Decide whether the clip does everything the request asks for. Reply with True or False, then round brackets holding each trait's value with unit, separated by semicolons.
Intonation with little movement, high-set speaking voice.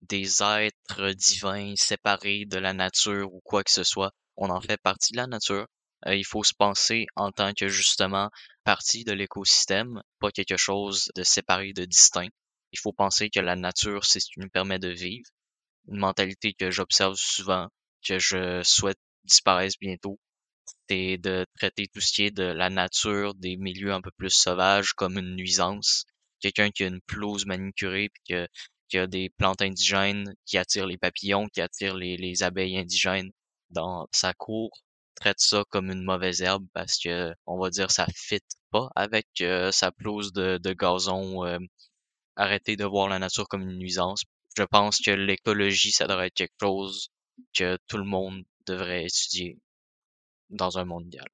False (1.5 semitones; 95 Hz)